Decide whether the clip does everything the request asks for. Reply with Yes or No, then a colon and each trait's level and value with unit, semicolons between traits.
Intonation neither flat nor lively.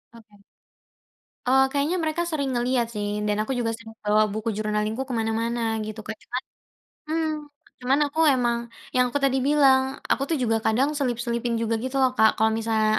Yes: average, 3.2 semitones